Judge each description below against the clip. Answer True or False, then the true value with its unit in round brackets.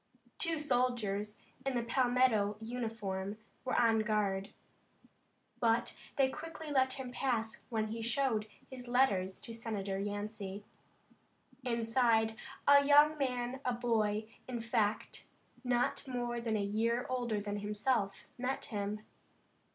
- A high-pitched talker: True (230 Hz)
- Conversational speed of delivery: False (125 wpm)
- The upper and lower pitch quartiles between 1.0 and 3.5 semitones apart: True (3.2 semitones)